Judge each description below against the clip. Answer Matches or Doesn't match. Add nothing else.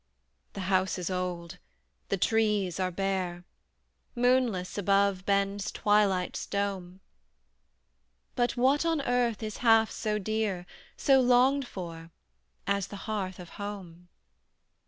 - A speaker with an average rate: Doesn't match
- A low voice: Doesn't match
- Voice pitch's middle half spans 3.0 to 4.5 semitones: Matches